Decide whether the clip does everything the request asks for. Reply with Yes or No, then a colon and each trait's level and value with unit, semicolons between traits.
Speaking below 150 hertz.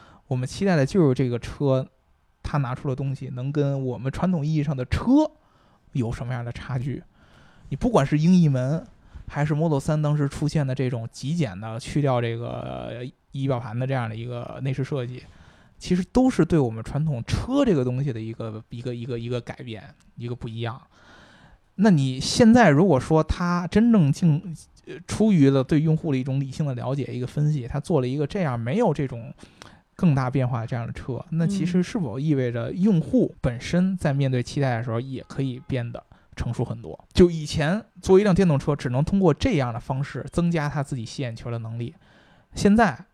Yes: medium, 140 Hz